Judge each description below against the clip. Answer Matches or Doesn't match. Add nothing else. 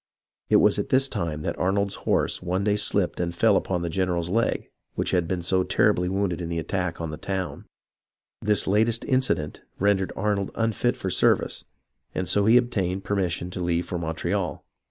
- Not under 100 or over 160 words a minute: Doesn't match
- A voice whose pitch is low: Matches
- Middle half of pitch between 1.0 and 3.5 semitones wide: Matches